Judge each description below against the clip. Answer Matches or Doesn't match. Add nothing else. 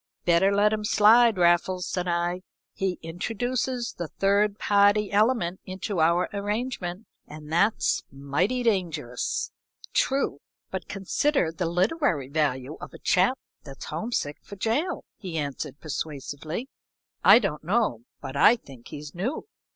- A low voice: Doesn't match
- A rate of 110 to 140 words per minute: Matches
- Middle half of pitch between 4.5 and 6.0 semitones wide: Matches